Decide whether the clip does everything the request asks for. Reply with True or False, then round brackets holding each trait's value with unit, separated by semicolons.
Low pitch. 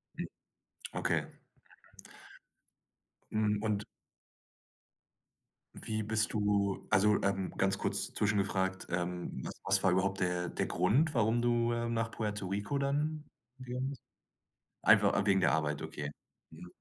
True (105 Hz)